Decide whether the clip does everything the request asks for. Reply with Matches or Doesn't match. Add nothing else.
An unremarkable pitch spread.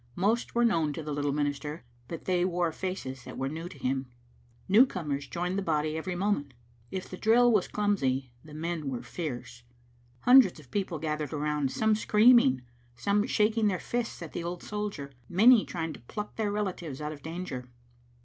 Doesn't match